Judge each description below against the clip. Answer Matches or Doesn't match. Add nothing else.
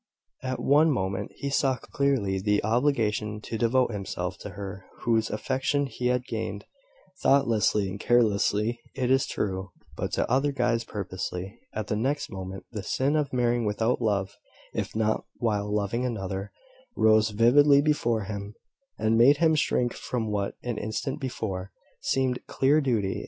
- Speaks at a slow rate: Doesn't match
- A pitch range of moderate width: Matches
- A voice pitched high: Doesn't match